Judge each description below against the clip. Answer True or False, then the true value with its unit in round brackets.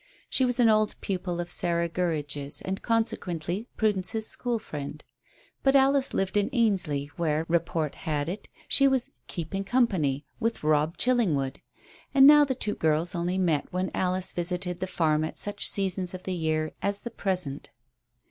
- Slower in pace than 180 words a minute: True (165 wpm)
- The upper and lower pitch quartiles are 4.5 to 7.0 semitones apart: True (5.3 semitones)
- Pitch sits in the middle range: True (180 Hz)